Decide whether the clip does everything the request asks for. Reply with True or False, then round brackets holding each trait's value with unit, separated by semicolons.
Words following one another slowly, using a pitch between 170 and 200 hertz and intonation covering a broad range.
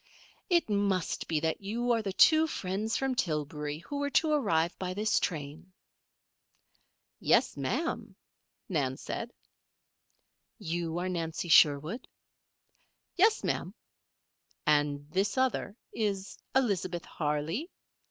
True (115 wpm; 185 Hz; 6.5 semitones)